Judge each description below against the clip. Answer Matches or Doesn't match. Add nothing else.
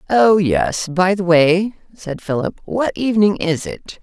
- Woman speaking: Matches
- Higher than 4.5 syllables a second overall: Doesn't match